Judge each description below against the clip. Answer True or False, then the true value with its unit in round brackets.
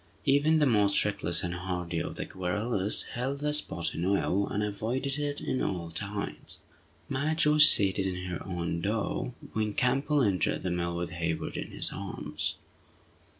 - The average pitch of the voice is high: False (100 Hz)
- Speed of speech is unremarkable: True (165 wpm)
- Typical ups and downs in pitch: False (6.9 semitones)